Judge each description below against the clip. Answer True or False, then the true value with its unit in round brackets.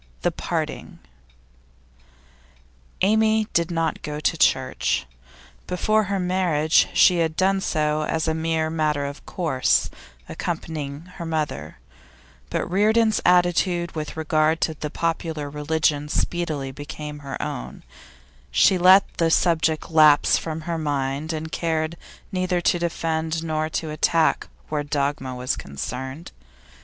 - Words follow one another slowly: True (125 wpm)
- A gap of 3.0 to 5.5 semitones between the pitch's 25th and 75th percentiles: False (2.6 semitones)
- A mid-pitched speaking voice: True (160 Hz)